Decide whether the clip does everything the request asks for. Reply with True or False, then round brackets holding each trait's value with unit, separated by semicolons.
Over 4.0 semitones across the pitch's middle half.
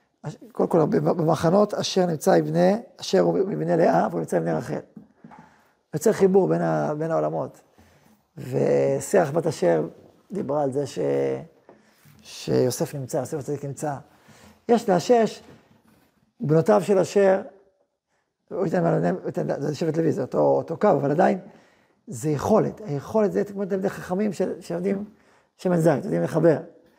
True (5.5 semitones)